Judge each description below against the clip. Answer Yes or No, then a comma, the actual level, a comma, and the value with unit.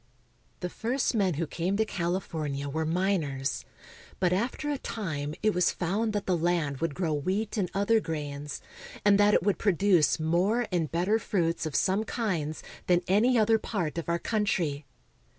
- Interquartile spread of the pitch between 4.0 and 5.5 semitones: Yes, average, 4.5 semitones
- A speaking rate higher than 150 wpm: Yes, average, 180 wpm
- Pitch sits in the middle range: Yes, medium, 180 Hz